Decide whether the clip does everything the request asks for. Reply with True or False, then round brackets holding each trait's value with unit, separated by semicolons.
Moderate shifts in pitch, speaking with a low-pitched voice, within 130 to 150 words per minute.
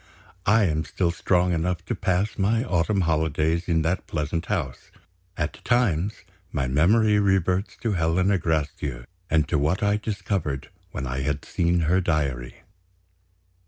True (4.0 semitones; 85 Hz; 145 wpm)